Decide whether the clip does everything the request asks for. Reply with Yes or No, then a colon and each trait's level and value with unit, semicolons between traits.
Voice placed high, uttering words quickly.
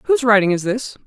Yes: high, 225 Hz; fast, 225 wpm